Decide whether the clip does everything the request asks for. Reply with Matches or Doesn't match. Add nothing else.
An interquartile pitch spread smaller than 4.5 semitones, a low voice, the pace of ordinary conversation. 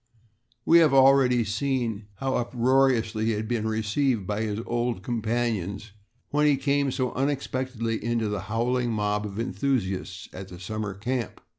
Matches